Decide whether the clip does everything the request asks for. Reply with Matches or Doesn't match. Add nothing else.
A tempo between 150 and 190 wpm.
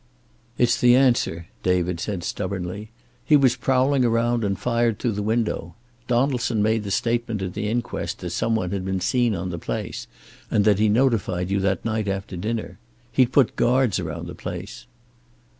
Matches